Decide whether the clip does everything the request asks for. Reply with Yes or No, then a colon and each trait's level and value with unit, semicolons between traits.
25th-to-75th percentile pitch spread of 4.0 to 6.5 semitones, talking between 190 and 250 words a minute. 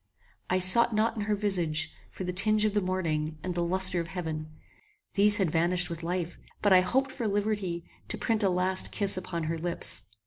No: average, 3.3 semitones; fast, 205 wpm